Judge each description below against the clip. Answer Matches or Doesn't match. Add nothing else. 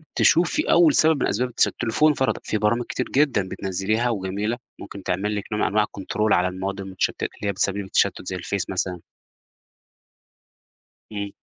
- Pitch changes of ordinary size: Matches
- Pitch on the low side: Matches